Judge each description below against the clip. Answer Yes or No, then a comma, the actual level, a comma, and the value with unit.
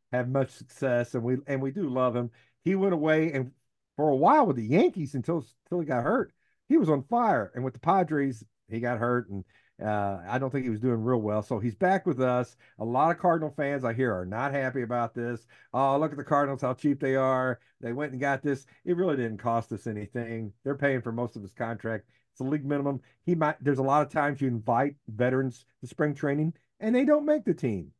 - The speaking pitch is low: Yes, low, 130 Hz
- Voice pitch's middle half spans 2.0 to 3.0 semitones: No, average, 3.5 semitones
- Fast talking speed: Yes, fast, 240 wpm